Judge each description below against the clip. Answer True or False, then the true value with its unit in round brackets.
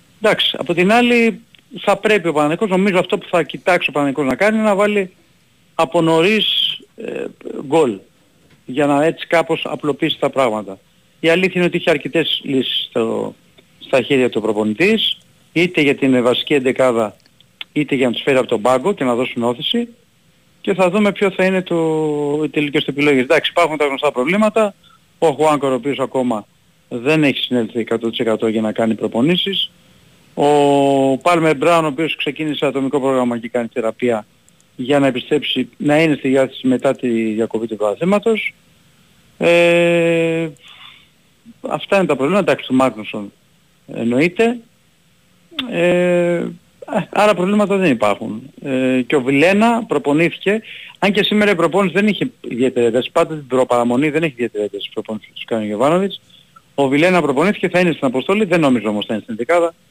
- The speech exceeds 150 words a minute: True (165 wpm)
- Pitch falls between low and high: True (155 Hz)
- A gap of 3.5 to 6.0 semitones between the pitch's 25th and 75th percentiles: True (5.6 semitones)